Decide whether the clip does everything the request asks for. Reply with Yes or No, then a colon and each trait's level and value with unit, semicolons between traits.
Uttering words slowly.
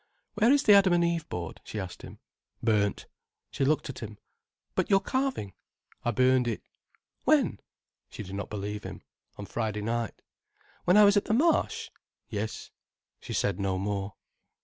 No: average, 170 wpm